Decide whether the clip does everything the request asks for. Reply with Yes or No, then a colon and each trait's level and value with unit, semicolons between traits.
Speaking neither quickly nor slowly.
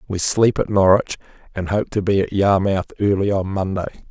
Yes: average, 190 wpm